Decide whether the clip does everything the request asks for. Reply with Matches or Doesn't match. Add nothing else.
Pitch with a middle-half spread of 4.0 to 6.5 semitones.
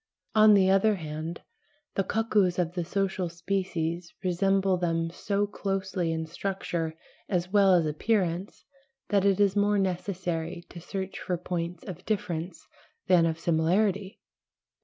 Doesn't match